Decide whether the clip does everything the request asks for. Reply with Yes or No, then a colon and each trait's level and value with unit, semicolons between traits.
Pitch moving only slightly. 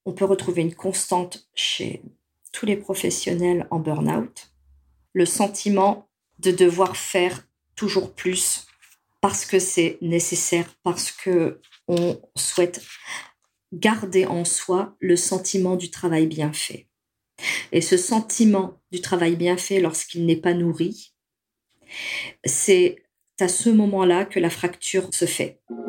Yes: narrow, 1.9 semitones